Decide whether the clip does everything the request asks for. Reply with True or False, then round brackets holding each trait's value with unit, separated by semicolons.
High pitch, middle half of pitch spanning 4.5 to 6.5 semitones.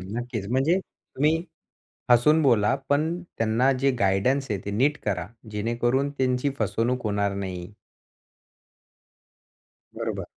False (120 Hz; 5.0 semitones)